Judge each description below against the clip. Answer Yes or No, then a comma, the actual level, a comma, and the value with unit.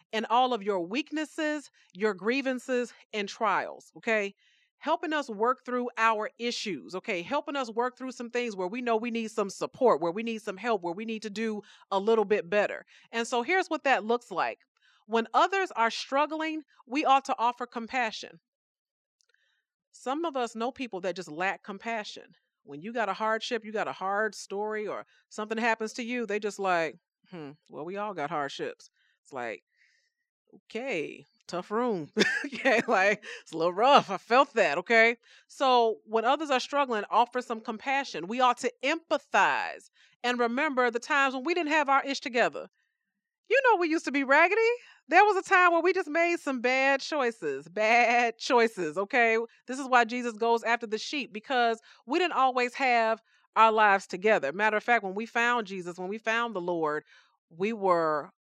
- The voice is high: Yes, high, 235 Hz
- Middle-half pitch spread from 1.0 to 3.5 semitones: No, average, 4.2 semitones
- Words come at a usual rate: Yes, average, 185 wpm